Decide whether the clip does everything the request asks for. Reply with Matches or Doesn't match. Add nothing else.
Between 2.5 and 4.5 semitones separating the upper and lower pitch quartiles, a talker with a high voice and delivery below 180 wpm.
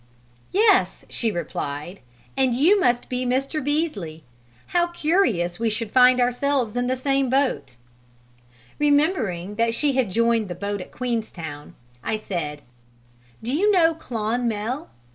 Doesn't match